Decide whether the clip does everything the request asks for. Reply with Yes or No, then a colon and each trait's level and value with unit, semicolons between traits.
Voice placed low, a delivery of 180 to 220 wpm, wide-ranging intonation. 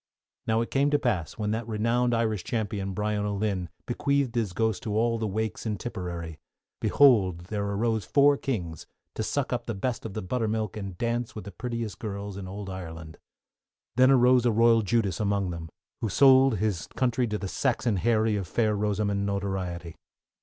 No: low, 110 Hz; average, 185 wpm; average, 3.2 semitones